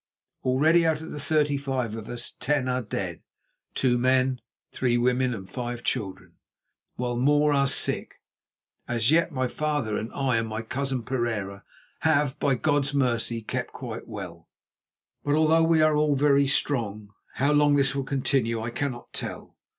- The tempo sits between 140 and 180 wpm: Yes, average, 165 wpm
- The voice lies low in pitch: Yes, low, 130 Hz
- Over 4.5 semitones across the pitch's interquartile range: No, average, 3.7 semitones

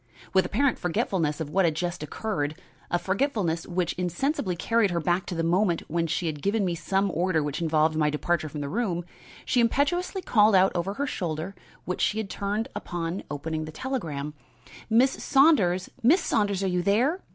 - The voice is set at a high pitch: No, medium, 180 Hz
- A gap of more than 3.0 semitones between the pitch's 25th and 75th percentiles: Yes, average, 4.9 semitones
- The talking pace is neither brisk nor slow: Yes, average, 185 wpm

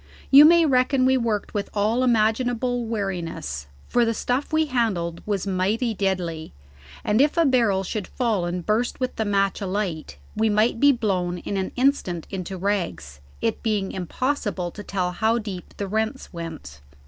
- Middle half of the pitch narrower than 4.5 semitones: No, average, 4.9 semitones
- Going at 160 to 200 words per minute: Yes, average, 170 wpm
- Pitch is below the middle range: No, high, 210 Hz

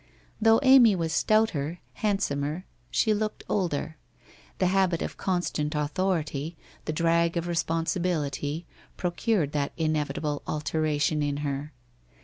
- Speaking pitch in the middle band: Yes, medium, 165 Hz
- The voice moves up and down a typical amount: Yes, average, 3.8 semitones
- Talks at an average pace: No, slow, 115 wpm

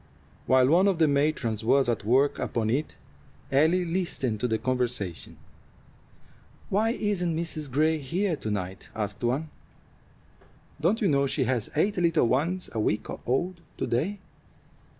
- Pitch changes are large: Yes, wide, 6.1 semitones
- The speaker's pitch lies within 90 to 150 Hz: Yes, medium, 140 Hz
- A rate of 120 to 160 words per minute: Yes, average, 150 wpm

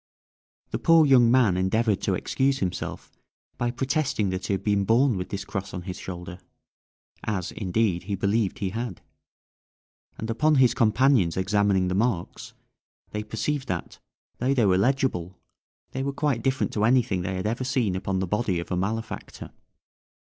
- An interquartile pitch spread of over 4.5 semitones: Yes, average, 5.1 semitones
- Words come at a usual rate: Yes, average, 170 wpm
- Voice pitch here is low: Yes, low, 105 Hz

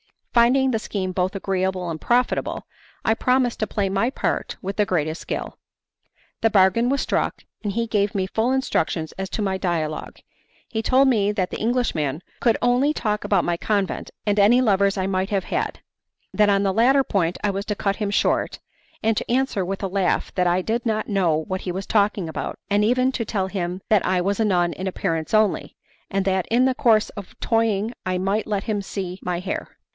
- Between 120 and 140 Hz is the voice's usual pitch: No, high, 200 Hz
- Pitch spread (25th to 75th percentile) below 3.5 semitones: Yes, average, 3.1 semitones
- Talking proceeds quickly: Yes, fast, 210 wpm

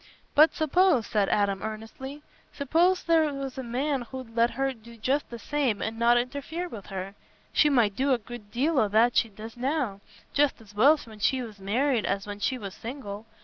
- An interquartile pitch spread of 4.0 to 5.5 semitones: Yes, average, 4.6 semitones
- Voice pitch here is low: No, high, 240 Hz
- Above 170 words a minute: Yes, average, 200 wpm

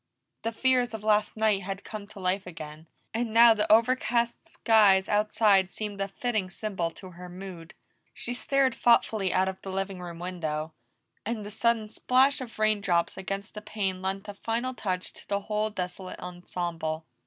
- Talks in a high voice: Yes, high, 200 Hz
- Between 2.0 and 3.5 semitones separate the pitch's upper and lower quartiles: Yes, average, 3.2 semitones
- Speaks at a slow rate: No, average, 175 wpm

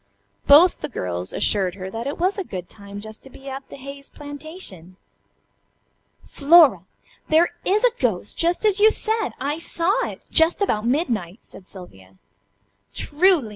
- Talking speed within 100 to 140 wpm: No, average, 160 wpm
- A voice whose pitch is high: Yes, very high, 275 Hz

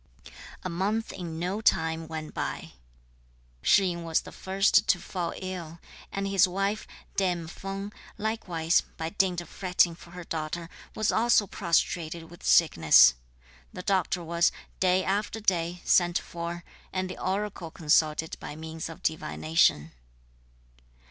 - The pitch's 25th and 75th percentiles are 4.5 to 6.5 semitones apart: No, average, 2.9 semitones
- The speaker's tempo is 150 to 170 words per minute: No, average, 140 wpm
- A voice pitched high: No, medium, 175 Hz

